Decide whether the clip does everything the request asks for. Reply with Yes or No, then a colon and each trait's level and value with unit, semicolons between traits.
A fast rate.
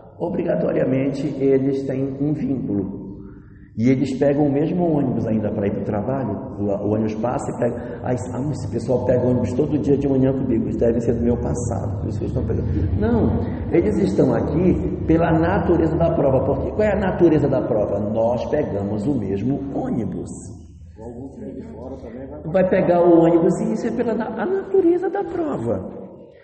No: average, 155 wpm